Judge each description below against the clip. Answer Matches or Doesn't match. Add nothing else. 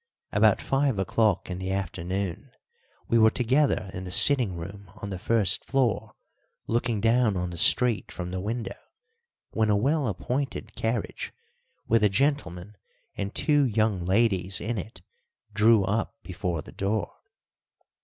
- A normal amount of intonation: Matches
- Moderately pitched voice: Doesn't match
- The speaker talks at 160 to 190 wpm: Doesn't match